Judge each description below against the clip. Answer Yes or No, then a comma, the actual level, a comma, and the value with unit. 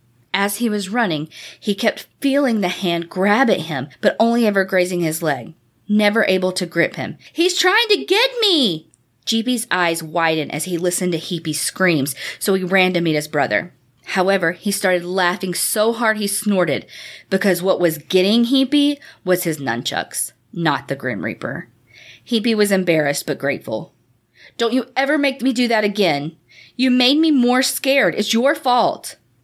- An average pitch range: No, wide, 6.1 semitones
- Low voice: No, high, 190 Hz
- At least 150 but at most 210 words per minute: Yes, average, 175 wpm